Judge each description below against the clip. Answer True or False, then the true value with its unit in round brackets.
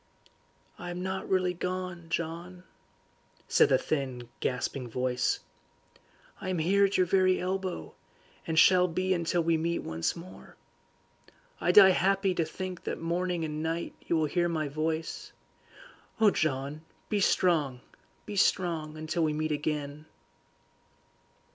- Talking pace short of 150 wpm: True (140 wpm)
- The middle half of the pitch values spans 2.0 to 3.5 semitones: True (3.0 semitones)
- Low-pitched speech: False (170 Hz)